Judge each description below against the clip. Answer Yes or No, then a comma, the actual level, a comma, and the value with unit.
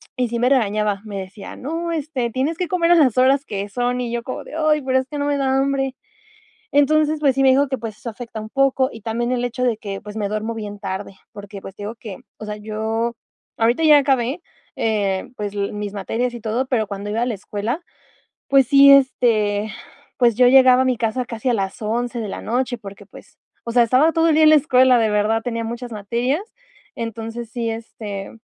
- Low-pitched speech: No, high, 235 Hz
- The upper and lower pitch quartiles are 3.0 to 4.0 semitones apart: Yes, average, 3.7 semitones